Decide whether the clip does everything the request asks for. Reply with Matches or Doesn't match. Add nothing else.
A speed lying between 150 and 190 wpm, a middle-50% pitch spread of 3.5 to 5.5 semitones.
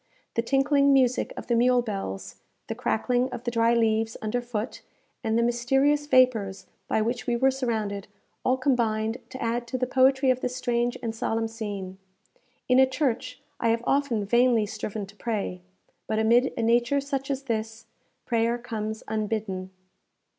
Doesn't match